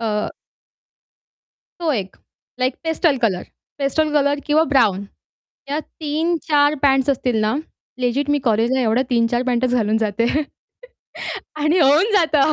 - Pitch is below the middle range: No, very high, 270 Hz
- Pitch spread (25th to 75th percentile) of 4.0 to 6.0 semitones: Yes, average, 4.4 semitones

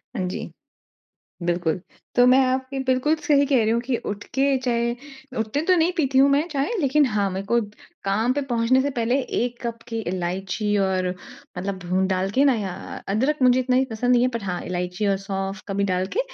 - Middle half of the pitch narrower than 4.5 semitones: No, average, 5.3 semitones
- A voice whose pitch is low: No, high, 230 Hz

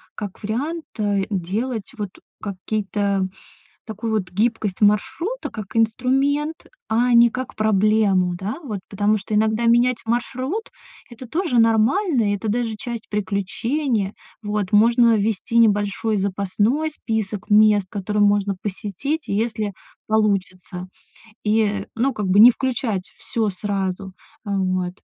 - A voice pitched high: Yes, high, 215 Hz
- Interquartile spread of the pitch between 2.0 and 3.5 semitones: Yes, average, 2.8 semitones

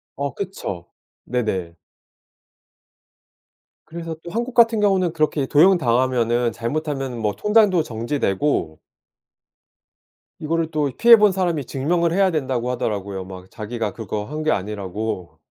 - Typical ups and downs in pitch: No, wide, 7.8 semitones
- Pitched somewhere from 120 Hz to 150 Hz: Yes, low, 135 Hz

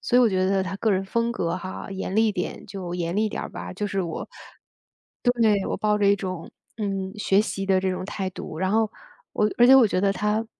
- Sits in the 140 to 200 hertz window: Yes, high, 195 Hz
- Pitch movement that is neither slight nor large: No, narrow, 2.2 semitones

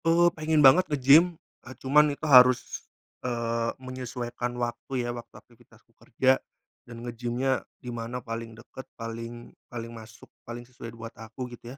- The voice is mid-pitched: No, low, 120 Hz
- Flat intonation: Yes, narrow, 2.1 semitones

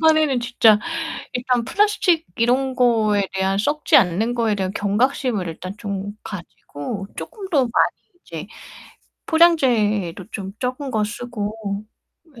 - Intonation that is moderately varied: Yes, average, 4.7 semitones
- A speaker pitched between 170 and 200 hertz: No, high, 235 Hz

